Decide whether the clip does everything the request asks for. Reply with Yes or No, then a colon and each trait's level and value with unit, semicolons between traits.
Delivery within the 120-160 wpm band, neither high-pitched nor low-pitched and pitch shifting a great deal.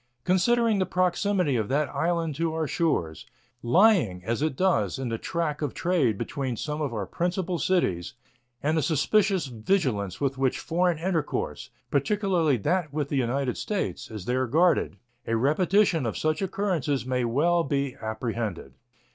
Yes: average, 155 wpm; medium, 150 Hz; wide, 6.2 semitones